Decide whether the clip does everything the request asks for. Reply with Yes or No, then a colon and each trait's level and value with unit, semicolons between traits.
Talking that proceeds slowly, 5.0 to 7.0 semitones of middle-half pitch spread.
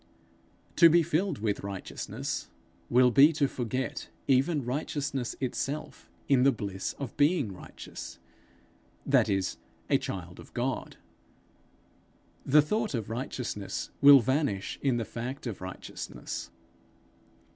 No: slow, 120 wpm; average, 4.4 semitones